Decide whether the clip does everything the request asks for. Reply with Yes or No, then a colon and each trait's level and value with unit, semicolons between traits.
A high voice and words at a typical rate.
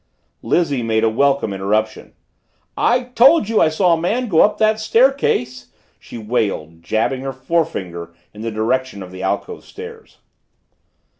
No: low, 130 Hz; average, 150 wpm